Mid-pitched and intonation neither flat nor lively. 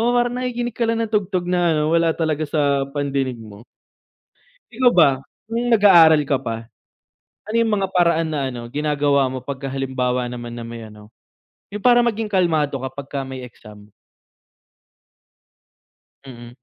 No: medium, 150 Hz; wide, 7.6 semitones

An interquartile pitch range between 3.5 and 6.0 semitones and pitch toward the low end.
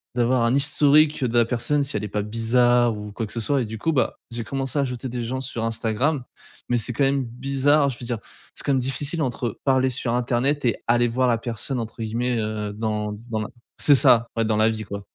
No: average, 3.0 semitones; low, 120 Hz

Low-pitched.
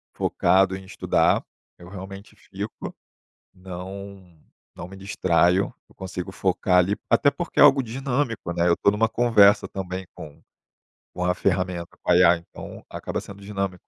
Yes: very low, 95 Hz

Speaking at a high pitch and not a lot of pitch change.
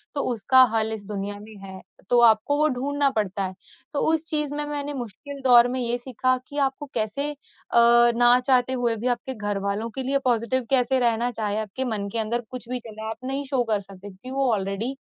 No: high, 240 Hz; average, 3.3 semitones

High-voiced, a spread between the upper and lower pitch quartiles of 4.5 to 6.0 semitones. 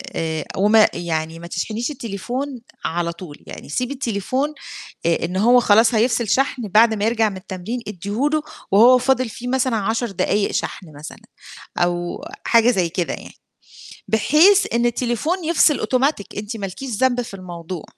Yes: high, 220 Hz; average, 5.2 semitones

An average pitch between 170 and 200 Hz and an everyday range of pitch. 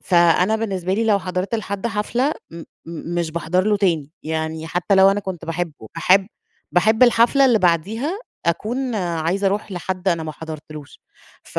Yes: medium, 185 Hz; average, 4.1 semitones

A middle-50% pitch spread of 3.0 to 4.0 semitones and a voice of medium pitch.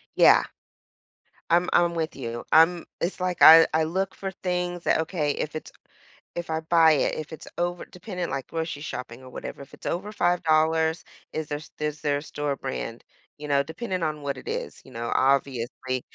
Yes: average, 3.5 semitones; medium, 160 Hz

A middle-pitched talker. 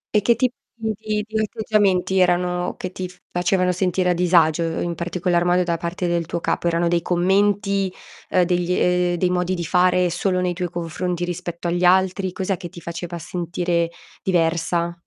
Yes: medium, 180 Hz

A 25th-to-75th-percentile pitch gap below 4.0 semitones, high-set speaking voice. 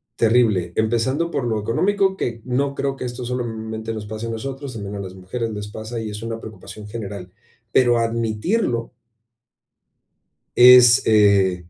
No: average, 2.8 semitones; low, 115 Hz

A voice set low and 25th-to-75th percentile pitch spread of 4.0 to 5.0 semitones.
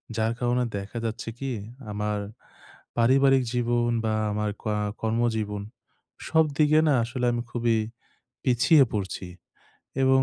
No: low, 120 Hz; average, 3.2 semitones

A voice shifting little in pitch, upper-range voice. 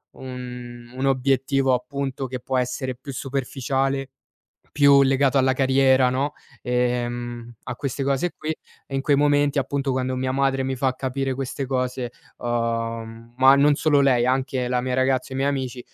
No: narrow, 1.6 semitones; low, 130 Hz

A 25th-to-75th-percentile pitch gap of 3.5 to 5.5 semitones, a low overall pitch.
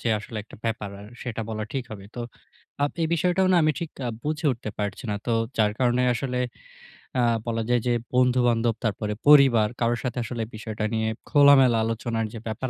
No: average, 2.8 semitones; low, 120 Hz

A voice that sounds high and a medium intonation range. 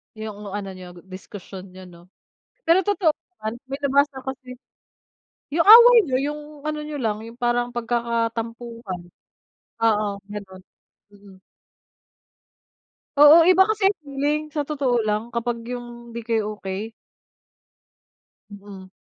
No: high, 235 Hz; wide, 5.7 semitones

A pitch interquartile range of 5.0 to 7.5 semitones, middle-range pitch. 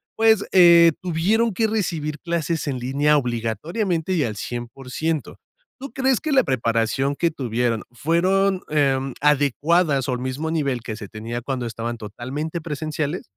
Yes: wide, 5.6 semitones; medium, 150 Hz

